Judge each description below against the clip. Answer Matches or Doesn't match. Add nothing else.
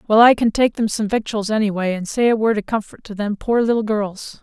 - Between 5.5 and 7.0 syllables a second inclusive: Matches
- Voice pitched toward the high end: Matches